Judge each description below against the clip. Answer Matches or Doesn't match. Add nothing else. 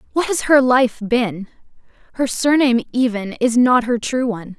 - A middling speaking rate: Matches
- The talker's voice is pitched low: Doesn't match